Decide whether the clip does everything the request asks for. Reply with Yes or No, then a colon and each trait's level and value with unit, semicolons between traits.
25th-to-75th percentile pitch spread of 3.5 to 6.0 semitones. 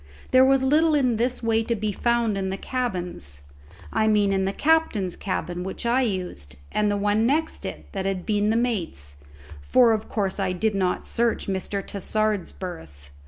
Yes: average, 3.9 semitones